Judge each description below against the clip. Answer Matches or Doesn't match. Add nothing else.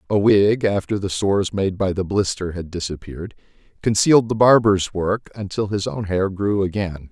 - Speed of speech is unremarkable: Matches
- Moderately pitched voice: Doesn't match